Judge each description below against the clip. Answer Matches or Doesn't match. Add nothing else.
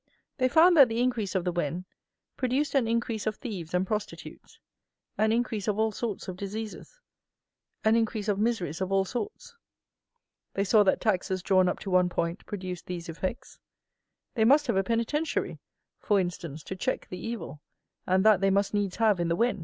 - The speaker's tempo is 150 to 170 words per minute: Doesn't match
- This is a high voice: Matches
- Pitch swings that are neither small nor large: Matches